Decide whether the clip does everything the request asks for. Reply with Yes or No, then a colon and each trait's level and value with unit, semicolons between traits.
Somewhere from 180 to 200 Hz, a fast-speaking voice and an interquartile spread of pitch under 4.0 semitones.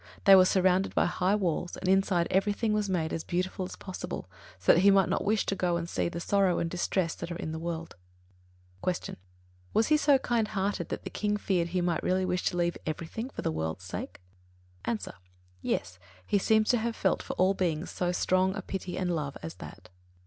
Yes: medium, 185 Hz; fast, 220 wpm; narrow, 2.6 semitones